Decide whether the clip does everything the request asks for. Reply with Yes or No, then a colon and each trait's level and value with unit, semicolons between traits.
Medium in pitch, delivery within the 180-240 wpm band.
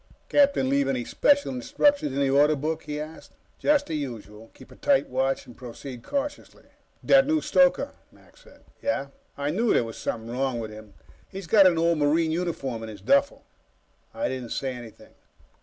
Yes: medium, 145 Hz; average, 185 wpm